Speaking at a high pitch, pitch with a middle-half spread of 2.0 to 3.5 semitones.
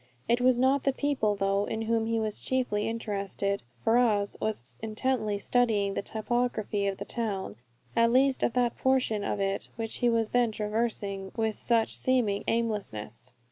Yes: high, 220 Hz; average, 3.1 semitones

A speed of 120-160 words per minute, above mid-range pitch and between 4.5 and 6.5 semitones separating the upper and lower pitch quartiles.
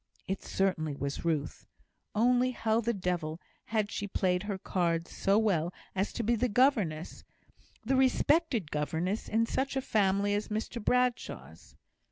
Yes: average, 150 wpm; high, 205 Hz; average, 5.1 semitones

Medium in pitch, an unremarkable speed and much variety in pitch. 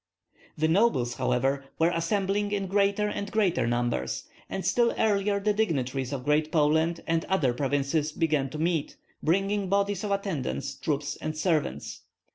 Yes: medium, 165 Hz; average, 150 wpm; wide, 6.0 semitones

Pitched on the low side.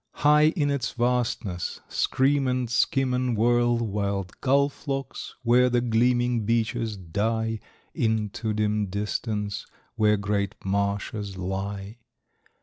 Yes: low, 115 Hz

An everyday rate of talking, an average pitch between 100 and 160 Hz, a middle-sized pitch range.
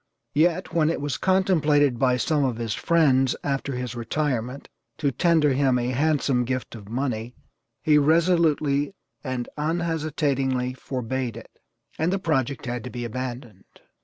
Yes: average, 145 wpm; low, 135 Hz; average, 3.8 semitones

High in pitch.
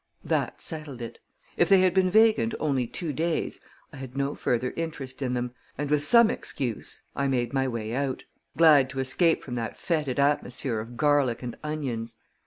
No: medium, 140 Hz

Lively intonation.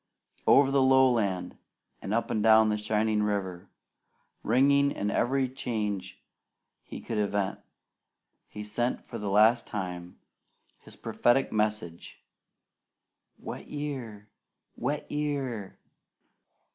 No: average, 4.2 semitones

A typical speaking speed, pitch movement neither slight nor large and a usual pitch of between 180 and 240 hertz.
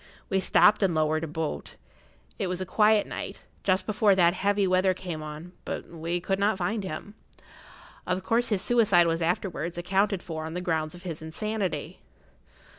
Yes: average, 180 wpm; average, 3.3 semitones; medium, 185 Hz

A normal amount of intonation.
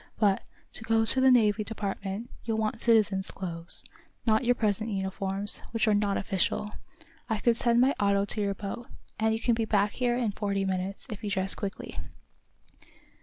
No: narrow, 2.3 semitones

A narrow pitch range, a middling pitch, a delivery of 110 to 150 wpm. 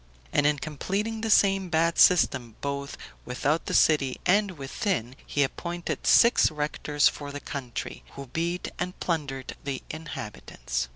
No: average, 4.5 semitones; medium, 150 Hz; average, 140 wpm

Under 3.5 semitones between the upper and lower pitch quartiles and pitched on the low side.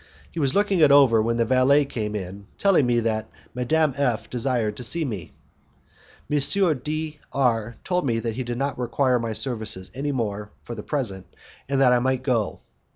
No: average, 3.8 semitones; low, 125 Hz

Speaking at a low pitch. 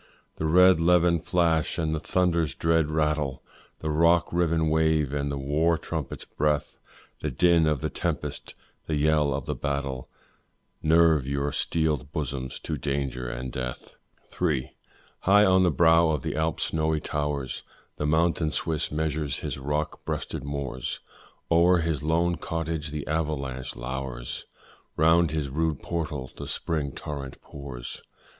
Yes: very low, 75 Hz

